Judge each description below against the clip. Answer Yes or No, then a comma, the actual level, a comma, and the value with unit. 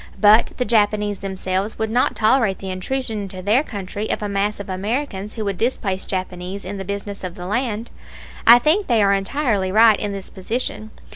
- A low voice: No, high, 205 Hz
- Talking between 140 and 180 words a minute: No, average, 195 wpm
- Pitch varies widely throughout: No, average, 2.7 semitones